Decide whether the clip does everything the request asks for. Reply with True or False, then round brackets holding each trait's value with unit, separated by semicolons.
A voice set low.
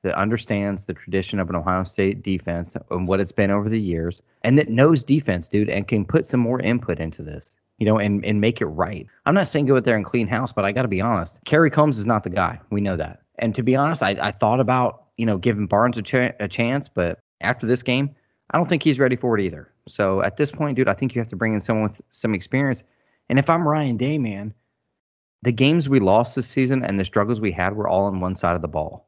True (110 Hz)